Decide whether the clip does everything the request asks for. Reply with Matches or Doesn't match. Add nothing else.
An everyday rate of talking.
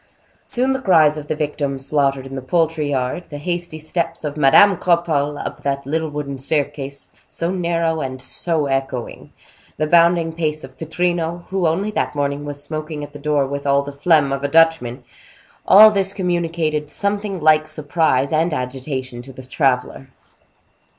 Matches